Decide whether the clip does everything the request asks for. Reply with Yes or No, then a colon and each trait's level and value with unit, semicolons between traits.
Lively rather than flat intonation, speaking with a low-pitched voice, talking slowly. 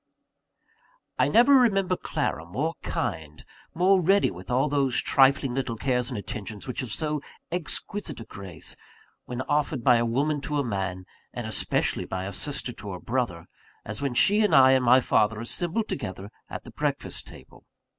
No: wide, 6.1 semitones; low, 130 Hz; average, 175 wpm